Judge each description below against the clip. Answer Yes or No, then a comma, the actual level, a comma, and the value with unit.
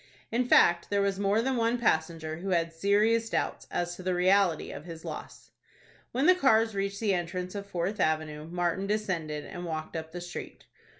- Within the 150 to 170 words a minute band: No, average, 190 wpm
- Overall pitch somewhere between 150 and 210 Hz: Yes, medium, 185 Hz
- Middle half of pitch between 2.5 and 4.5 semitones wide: Yes, average, 3.7 semitones